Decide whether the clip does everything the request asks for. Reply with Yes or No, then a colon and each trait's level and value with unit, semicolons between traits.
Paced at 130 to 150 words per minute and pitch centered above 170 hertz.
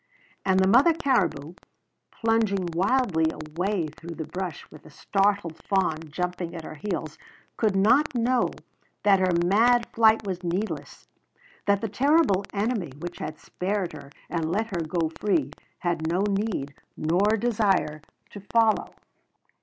Yes: average, 145 wpm; high, 190 Hz